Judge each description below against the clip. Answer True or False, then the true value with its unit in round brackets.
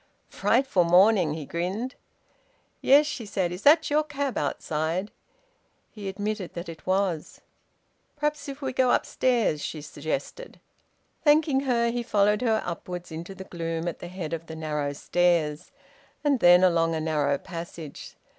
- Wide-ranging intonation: True (6.8 semitones)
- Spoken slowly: False (150 wpm)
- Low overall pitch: False (185 Hz)